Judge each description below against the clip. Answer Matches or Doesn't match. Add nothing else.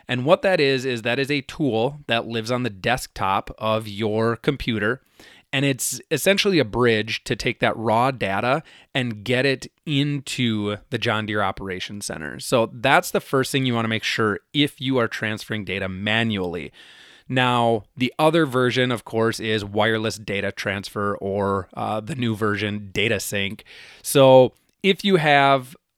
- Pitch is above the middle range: Doesn't match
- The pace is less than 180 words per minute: Matches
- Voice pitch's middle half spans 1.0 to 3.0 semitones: Doesn't match